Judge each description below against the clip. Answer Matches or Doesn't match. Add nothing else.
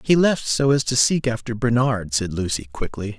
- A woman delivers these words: Doesn't match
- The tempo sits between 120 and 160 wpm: Doesn't match